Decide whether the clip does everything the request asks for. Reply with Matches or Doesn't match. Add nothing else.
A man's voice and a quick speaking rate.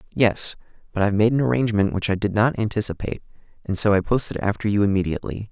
Doesn't match